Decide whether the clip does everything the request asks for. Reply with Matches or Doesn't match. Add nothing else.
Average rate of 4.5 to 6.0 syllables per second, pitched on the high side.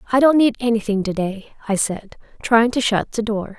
Matches